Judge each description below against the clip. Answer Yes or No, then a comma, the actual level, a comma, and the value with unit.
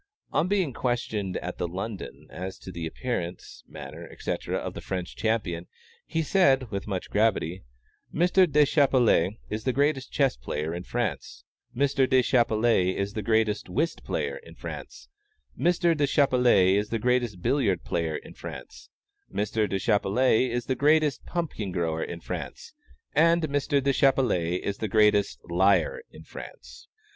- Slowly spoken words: No, average, 145 wpm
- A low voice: Yes, low, 115 Hz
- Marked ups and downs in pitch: Yes, wide, 6.5 semitones